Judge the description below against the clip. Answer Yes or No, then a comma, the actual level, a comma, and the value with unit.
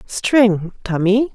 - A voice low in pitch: No, high, 215 Hz